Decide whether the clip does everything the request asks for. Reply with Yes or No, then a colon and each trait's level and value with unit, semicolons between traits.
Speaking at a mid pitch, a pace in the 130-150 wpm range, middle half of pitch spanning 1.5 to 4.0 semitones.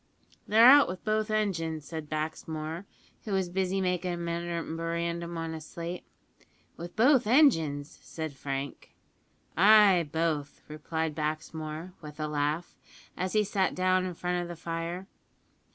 Yes: medium, 170 Hz; average, 140 wpm; average, 2.8 semitones